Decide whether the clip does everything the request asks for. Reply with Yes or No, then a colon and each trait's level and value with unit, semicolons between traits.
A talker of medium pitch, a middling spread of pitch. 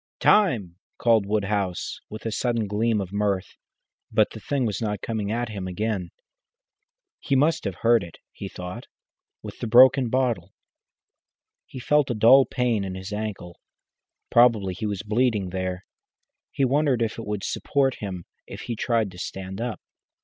No: low, 110 Hz; average, 3.8 semitones